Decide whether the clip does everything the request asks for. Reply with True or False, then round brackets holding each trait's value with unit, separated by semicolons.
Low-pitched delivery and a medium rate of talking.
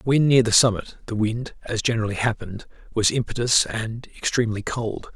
True (115 Hz; 165 wpm)